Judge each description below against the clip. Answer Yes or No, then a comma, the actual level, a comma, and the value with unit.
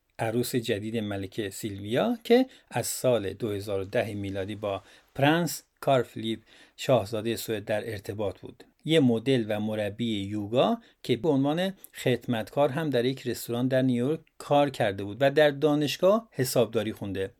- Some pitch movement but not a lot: Yes, average, 5.0 semitones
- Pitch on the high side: No, low, 120 Hz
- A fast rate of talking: No, average, 140 wpm